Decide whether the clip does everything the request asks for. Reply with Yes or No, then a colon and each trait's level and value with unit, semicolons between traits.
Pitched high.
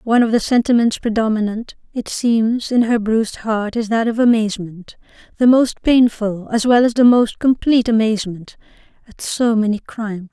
Yes: high, 225 Hz